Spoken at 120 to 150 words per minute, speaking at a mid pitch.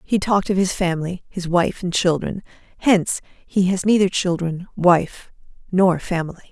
Yes: average, 145 wpm; medium, 180 Hz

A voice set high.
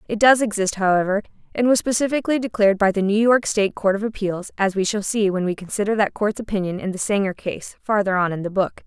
Yes: high, 205 Hz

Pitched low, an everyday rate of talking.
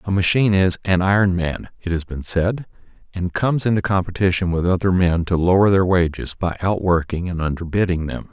Yes: very low, 90 Hz; average, 190 wpm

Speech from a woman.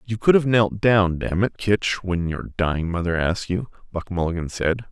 No: male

